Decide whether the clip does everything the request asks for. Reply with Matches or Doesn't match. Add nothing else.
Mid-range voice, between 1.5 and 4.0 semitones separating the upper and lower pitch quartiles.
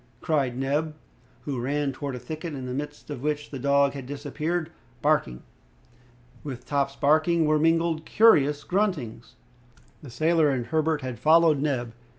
Matches